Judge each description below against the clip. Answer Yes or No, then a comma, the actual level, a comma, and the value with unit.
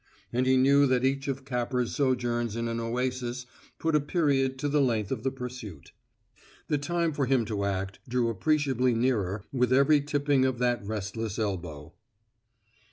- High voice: No, low, 125 Hz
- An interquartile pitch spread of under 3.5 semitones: Yes, average, 3.1 semitones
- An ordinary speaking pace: Yes, average, 165 wpm